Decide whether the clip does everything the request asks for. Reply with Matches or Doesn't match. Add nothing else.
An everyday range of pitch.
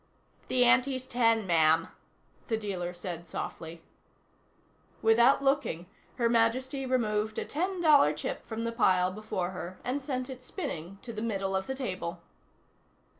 Doesn't match